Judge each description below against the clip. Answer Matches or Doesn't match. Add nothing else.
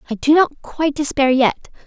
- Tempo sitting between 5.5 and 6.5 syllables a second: Doesn't match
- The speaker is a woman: Matches